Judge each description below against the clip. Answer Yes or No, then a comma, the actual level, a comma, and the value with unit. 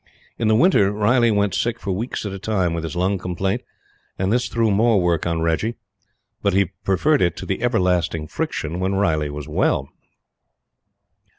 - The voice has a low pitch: Yes, very low, 95 Hz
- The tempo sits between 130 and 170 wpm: No, average, 180 wpm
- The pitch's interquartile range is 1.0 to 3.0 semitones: No, average, 4.0 semitones